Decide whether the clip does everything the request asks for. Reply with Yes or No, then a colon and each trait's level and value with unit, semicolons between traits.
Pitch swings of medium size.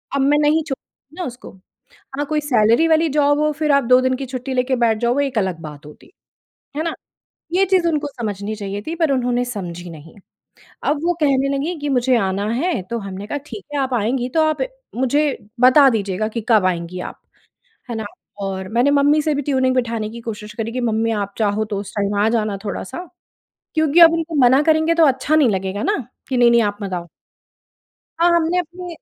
No: wide, 5.9 semitones